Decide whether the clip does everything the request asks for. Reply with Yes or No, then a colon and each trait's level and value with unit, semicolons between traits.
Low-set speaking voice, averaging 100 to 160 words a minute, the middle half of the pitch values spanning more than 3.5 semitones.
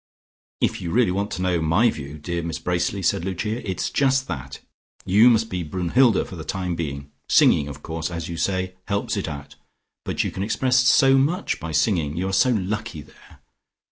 No: very low, 90 Hz; average, 195 wpm; average, 5.0 semitones